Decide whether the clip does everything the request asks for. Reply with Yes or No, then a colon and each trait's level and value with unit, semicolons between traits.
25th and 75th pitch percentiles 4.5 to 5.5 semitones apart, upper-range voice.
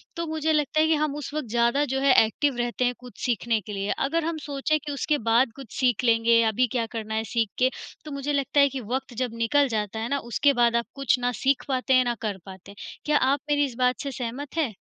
No: average, 3.6 semitones; very high, 255 Hz